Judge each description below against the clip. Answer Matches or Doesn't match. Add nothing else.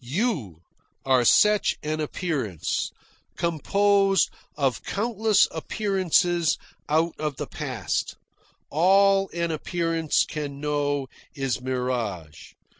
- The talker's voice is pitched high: Doesn't match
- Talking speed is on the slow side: Matches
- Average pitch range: Doesn't match